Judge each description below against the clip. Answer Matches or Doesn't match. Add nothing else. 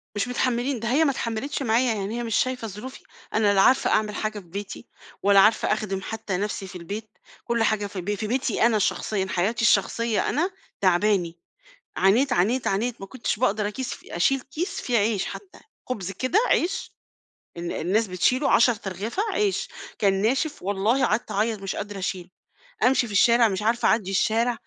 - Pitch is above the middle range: Matches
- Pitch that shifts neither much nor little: Matches